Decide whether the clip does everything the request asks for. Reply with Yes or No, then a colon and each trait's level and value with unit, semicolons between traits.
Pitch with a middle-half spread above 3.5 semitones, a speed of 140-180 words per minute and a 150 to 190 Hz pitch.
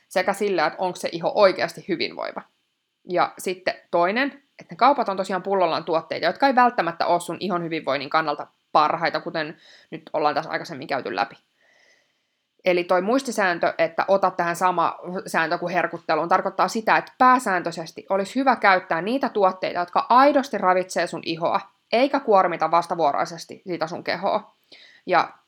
Yes: average, 4.8 semitones; fast, 155 wpm; medium, 185 Hz